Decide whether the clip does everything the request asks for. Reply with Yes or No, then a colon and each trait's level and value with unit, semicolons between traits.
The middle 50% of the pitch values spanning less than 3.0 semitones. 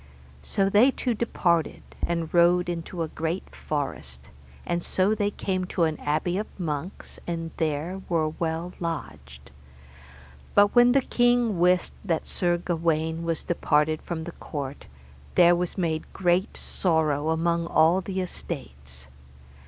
Yes: narrow, 2.6 semitones